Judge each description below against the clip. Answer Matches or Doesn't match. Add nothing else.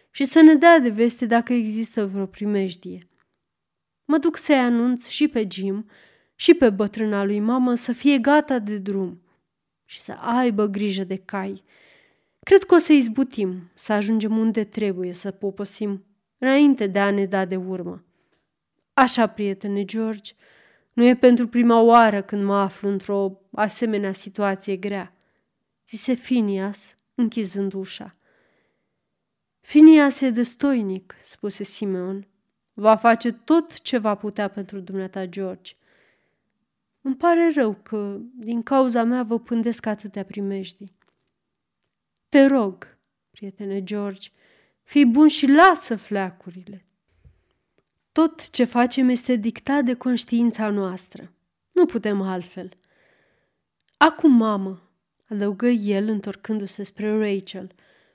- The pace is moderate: Matches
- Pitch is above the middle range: Matches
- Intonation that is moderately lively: Matches